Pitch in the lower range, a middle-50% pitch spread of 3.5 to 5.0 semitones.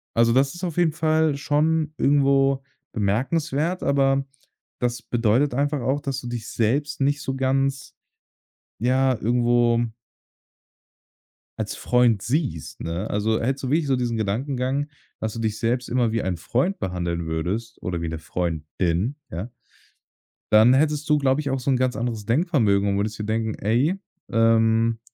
Yes: low, 125 Hz; average, 4.2 semitones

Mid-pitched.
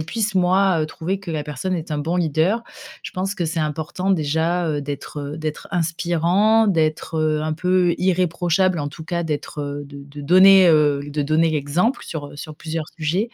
Yes: medium, 165 Hz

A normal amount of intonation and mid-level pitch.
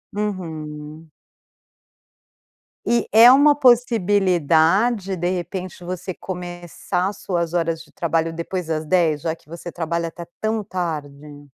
Yes: average, 3.0 semitones; medium, 175 Hz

